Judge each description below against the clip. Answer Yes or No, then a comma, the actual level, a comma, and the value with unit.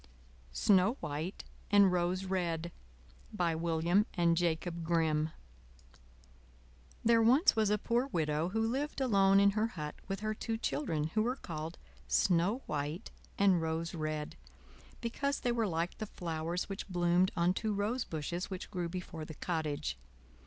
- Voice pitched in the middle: Yes, medium, 180 Hz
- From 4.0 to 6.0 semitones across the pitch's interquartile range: Yes, average, 4.6 semitones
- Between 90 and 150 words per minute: Yes, average, 145 wpm